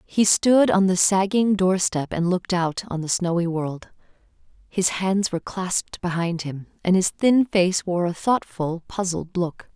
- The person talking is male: No, female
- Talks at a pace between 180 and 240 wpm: No, average, 170 wpm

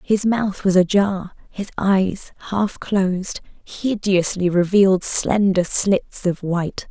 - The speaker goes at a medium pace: No, slow, 120 wpm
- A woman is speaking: Yes, female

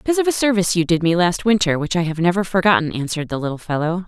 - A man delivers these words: No, female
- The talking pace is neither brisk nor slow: No, fast, 265 wpm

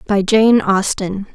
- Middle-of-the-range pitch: No, high, 205 Hz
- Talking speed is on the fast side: No, slow, 135 wpm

